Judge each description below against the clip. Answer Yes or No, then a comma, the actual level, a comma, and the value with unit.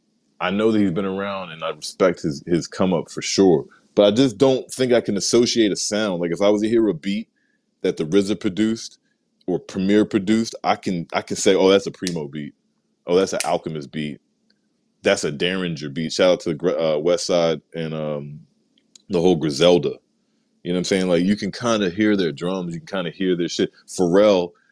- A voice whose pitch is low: Yes, very low, 95 Hz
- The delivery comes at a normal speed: No, fast, 225 wpm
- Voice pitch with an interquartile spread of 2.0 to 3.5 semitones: No, average, 4.2 semitones